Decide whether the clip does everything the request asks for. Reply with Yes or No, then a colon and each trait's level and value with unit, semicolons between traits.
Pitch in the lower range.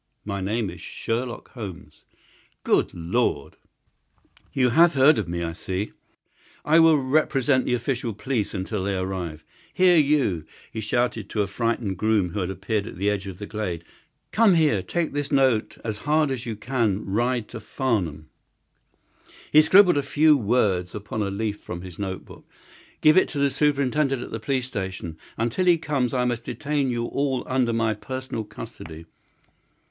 Yes: low, 115 Hz